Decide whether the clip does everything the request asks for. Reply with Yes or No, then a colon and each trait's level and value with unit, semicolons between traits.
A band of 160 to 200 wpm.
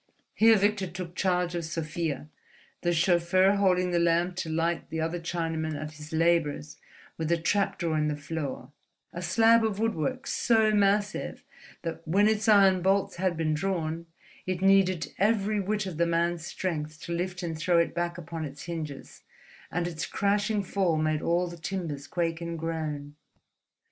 Yes: average, 170 wpm